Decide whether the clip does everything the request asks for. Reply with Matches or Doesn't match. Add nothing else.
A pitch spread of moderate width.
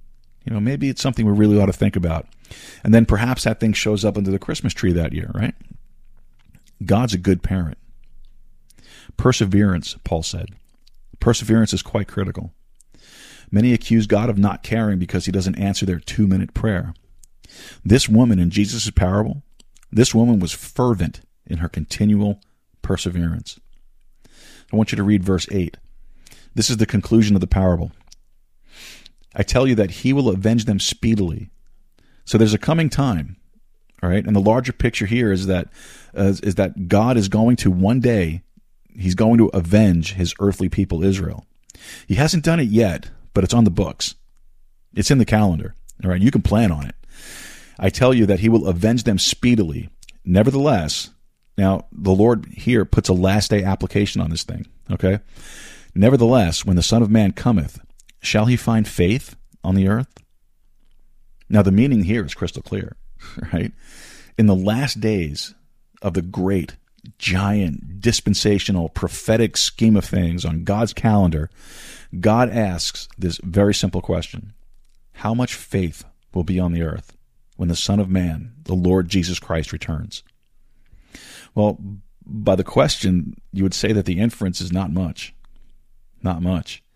Matches